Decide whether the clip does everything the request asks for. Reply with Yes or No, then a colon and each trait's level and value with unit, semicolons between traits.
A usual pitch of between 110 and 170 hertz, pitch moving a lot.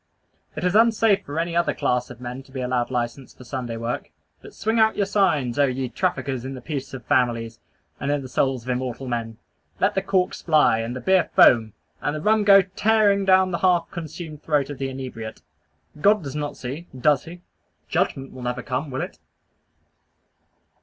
Yes: medium, 140 Hz; wide, 6.4 semitones